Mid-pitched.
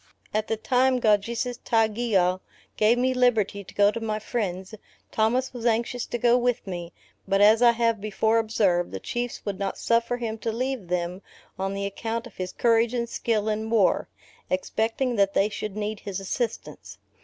No: high, 220 Hz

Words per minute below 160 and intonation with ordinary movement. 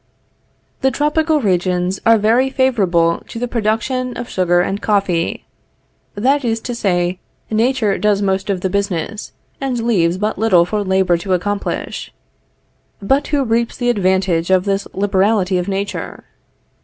Yes: average, 145 wpm; average, 4.0 semitones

